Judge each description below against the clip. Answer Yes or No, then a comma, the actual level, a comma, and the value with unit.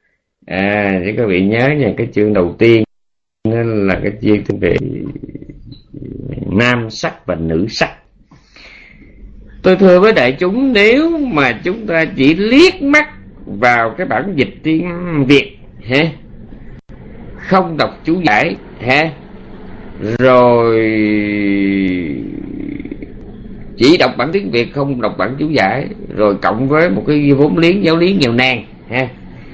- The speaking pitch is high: No, low, 130 Hz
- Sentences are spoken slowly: Yes, slow, 135 wpm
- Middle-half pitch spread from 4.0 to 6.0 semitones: No, wide, 7.2 semitones